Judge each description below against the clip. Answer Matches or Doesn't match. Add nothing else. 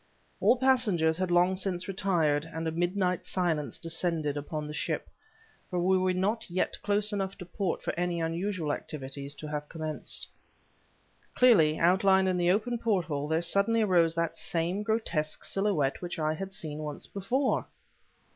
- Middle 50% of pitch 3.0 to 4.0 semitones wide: Matches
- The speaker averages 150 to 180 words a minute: Matches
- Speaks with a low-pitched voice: Doesn't match